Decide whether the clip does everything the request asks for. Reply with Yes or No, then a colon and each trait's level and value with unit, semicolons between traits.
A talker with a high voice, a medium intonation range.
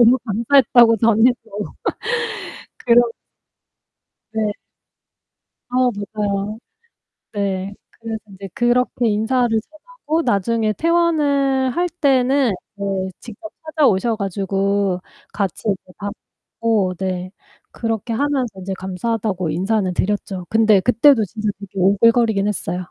Yes: high, 220 Hz; average, 4.1 semitones